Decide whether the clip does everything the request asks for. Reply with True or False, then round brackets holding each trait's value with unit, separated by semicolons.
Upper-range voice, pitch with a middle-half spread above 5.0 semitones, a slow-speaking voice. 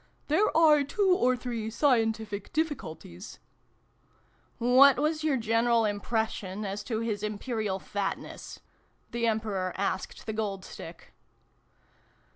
False (225 Hz; 4.2 semitones; 125 wpm)